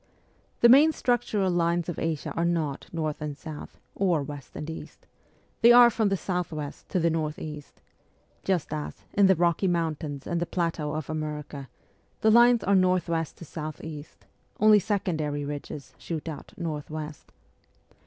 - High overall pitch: No, medium, 165 Hz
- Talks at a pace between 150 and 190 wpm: Yes, average, 170 wpm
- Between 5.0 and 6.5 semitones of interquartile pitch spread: No, average, 3.5 semitones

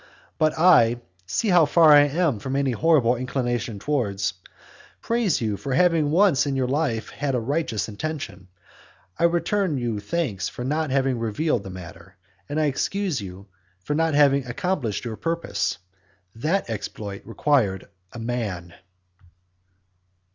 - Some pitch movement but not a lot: No, wide, 6.0 semitones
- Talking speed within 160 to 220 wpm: No, average, 145 wpm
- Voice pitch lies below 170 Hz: Yes, low, 135 Hz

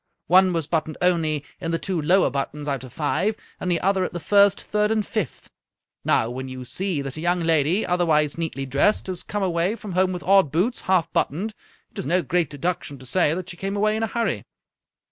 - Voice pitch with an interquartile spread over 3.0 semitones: Yes, average, 4.3 semitones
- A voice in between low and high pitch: Yes, medium, 175 Hz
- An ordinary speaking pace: No, fast, 220 wpm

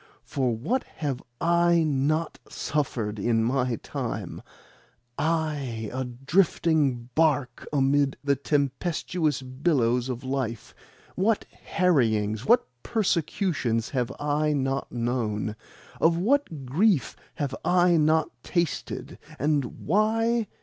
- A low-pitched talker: No, medium, 145 Hz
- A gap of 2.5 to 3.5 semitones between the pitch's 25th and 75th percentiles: No, average, 5.1 semitones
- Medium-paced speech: No, slow, 105 wpm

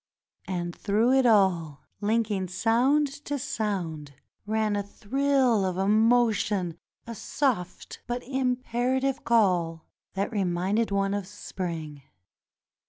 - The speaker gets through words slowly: Yes, slow, 105 wpm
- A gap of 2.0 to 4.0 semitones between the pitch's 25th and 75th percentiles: No, average, 4.7 semitones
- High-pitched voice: Yes, high, 210 Hz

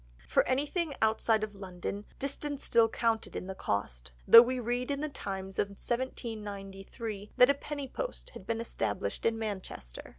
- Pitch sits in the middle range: No, high, 225 Hz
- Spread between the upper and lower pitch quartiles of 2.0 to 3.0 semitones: No, average, 4.8 semitones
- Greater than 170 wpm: No, average, 165 wpm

